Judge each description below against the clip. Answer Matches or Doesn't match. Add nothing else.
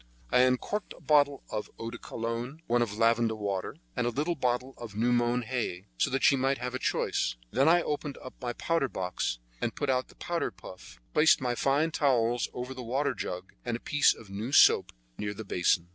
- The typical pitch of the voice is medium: Doesn't match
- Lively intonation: Doesn't match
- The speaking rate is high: Matches